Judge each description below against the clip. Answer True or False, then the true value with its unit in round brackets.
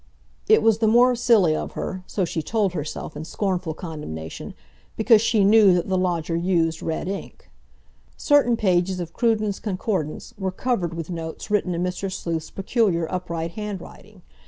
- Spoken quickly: False (155 wpm)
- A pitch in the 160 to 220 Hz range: True (185 Hz)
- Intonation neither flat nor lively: True (4.2 semitones)